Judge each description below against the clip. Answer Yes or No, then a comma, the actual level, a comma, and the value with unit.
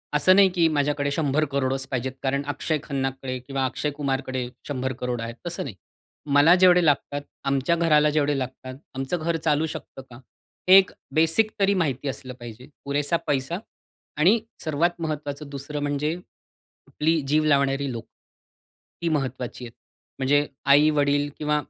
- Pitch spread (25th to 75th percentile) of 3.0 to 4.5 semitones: No, narrow, 2.6 semitones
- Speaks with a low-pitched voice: No, medium, 145 Hz